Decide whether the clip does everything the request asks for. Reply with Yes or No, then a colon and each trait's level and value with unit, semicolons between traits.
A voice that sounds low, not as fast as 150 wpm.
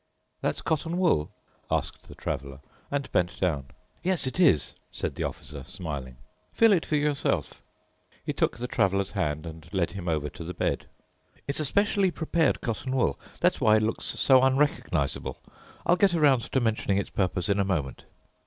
No: low, 105 Hz; average, 175 wpm